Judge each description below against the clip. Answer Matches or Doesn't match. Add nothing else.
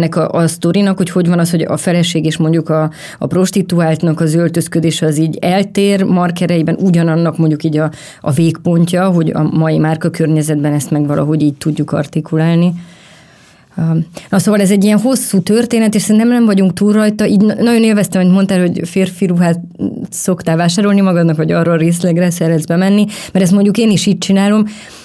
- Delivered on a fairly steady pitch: Doesn't match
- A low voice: Doesn't match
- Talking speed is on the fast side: Matches